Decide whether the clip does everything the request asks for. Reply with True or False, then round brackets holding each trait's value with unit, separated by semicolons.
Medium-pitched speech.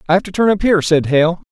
True (175 Hz)